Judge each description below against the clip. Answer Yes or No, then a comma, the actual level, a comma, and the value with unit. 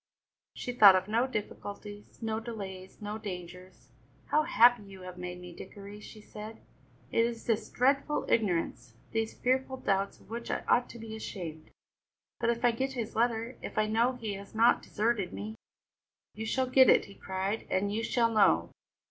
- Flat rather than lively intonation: No, average, 3.2 semitones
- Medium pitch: No, high, 220 Hz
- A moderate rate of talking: Yes, average, 180 wpm